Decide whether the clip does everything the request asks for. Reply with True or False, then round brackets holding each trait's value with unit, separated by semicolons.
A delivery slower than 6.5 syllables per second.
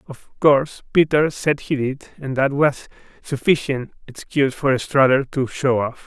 True (4.4 syllables/s)